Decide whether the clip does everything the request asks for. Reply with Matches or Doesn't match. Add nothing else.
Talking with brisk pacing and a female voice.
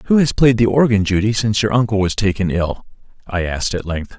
Doesn't match